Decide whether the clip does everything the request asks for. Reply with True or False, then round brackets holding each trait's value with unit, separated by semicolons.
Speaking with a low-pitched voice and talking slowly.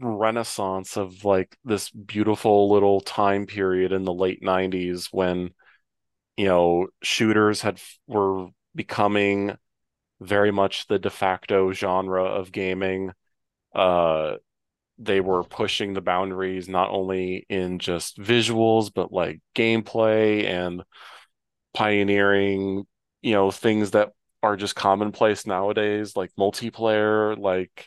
True (100 Hz; 115 wpm)